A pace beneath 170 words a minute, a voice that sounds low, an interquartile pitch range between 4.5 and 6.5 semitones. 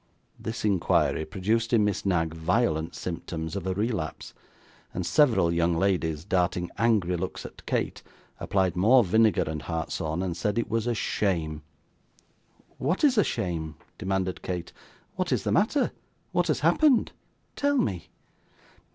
Yes: average, 145 wpm; very low, 95 Hz; average, 5.2 semitones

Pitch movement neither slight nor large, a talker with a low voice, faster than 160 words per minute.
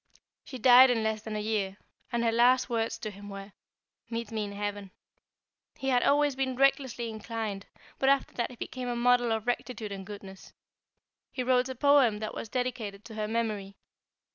No: average, 3.2 semitones; high, 230 Hz; average, 190 wpm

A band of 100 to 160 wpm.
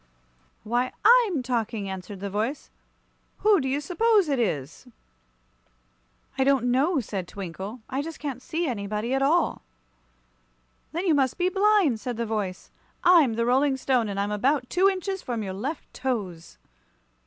Yes: average, 155 wpm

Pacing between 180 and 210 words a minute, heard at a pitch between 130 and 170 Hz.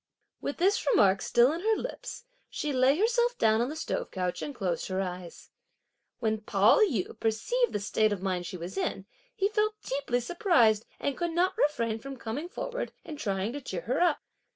No: average, 195 wpm; very high, 255 Hz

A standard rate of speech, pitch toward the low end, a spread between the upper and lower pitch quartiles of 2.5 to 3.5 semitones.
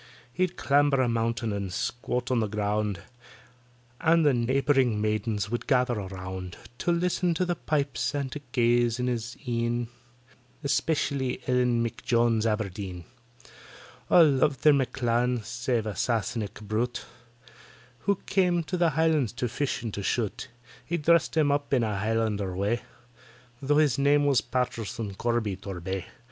No: average, 150 wpm; low, 120 Hz; average, 4.7 semitones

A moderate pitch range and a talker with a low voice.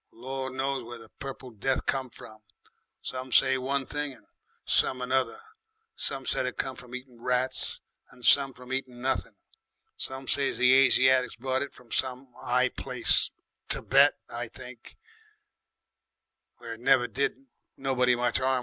No: narrow, 1.1 semitones; low, 130 Hz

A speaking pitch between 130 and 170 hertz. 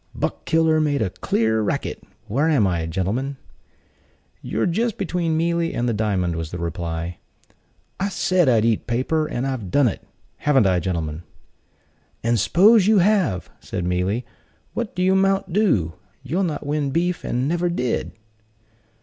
Yes: low, 135 Hz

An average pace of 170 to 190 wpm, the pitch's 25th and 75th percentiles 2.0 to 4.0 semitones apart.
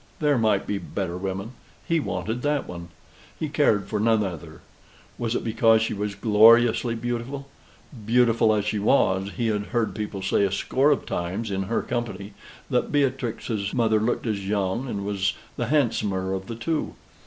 Yes: average, 175 wpm; average, 3.3 semitones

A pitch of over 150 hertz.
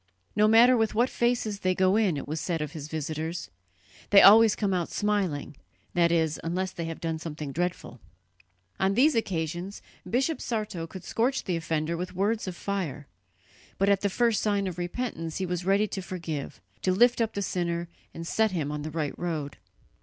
Yes: medium, 185 Hz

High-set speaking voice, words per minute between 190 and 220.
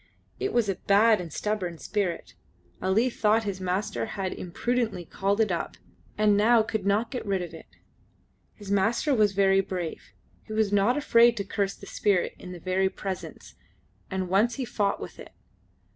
No: high, 200 Hz; average, 175 wpm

